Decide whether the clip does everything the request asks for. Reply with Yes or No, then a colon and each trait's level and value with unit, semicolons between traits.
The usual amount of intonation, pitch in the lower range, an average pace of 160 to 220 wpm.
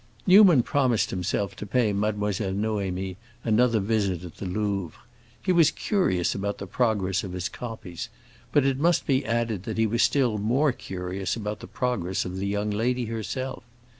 Yes: average, 4.4 semitones; low, 105 Hz; average, 170 wpm